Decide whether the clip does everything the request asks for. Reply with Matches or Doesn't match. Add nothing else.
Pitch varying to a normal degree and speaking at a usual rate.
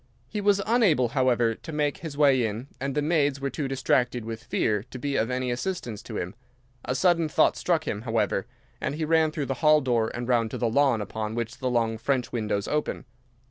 Doesn't match